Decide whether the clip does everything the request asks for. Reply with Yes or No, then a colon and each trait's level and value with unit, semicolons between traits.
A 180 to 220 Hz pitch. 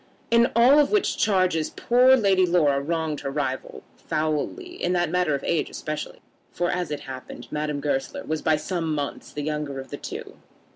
No: medium, 155 Hz